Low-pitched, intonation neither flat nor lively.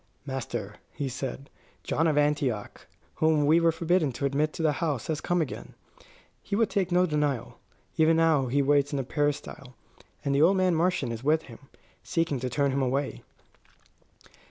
No: medium, 145 Hz; average, 3.1 semitones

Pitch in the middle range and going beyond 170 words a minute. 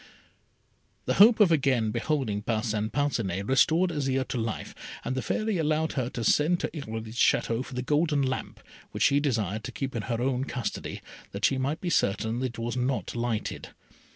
No: low, 130 Hz; average, 180 wpm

